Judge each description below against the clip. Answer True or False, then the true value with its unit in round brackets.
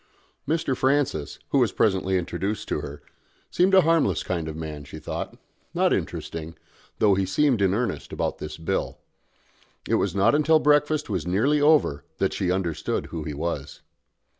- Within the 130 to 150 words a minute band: False (165 wpm)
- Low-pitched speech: True (95 Hz)